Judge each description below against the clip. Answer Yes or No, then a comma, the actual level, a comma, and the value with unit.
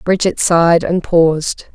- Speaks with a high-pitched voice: No, medium, 170 Hz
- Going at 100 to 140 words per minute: Yes, slow, 135 wpm